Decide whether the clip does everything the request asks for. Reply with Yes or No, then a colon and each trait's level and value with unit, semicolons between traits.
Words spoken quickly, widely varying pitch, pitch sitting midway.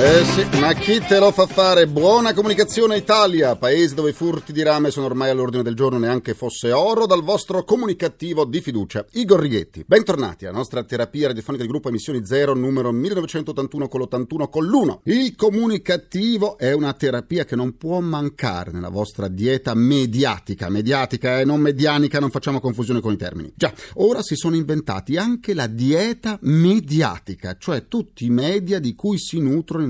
Yes: fast, 175 wpm; wide, 6.8 semitones; medium, 145 Hz